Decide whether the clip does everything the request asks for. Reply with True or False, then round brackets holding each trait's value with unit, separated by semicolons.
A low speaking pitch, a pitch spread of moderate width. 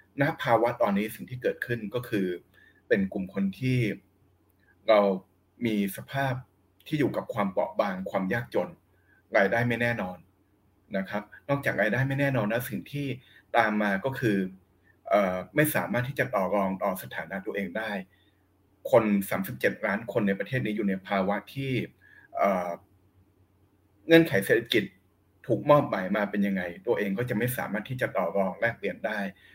True (100 Hz; 3.7 semitones)